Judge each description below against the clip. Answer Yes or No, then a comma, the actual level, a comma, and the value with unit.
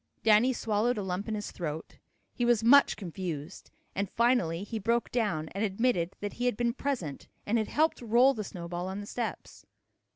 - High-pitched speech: Yes, high, 210 Hz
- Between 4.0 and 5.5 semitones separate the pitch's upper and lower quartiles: Yes, average, 4.5 semitones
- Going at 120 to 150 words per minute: No, average, 190 wpm